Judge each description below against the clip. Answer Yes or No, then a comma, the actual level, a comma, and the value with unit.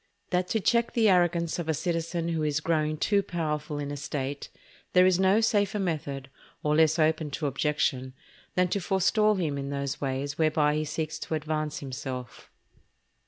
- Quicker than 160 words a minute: Yes, average, 175 wpm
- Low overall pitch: No, medium, 155 Hz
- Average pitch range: Yes, average, 3.7 semitones